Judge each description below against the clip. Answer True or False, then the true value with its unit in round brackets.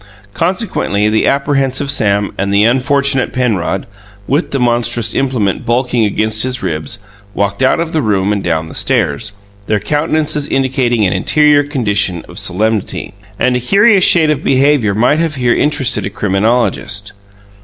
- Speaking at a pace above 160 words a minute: False (155 wpm)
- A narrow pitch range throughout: False (5.4 semitones)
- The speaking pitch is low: True (120 Hz)